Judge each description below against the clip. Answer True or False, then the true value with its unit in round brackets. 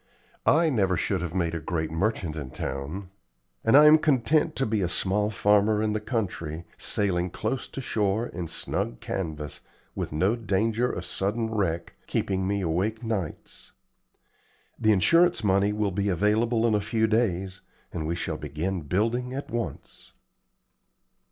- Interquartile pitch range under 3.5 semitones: False (4.3 semitones)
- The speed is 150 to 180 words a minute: True (160 wpm)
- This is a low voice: True (100 Hz)